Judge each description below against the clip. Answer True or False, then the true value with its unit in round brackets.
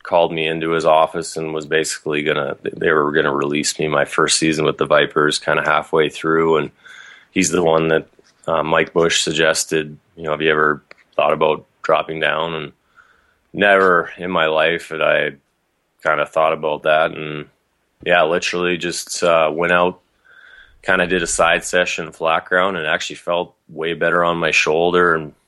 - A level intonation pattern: True (1.8 semitones)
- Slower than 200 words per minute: True (190 wpm)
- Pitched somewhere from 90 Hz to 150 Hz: False (80 Hz)